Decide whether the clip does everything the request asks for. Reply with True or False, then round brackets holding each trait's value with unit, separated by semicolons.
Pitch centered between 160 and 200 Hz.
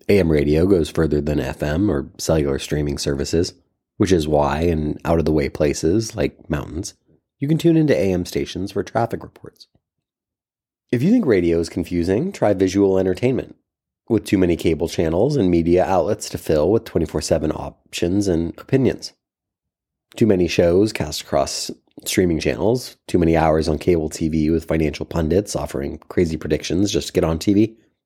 False (85 Hz)